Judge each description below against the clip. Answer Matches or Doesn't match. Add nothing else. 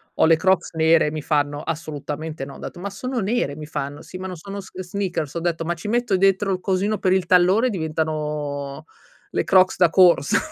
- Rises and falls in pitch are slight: Doesn't match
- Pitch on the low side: Doesn't match